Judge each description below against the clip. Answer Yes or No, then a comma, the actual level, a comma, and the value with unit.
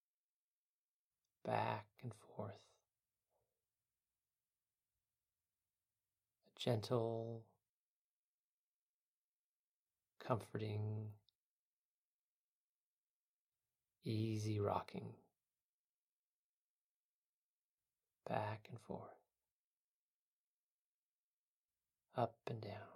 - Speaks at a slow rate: Yes, slow, 35 wpm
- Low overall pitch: Yes, low, 105 Hz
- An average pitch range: No, narrow, 1.8 semitones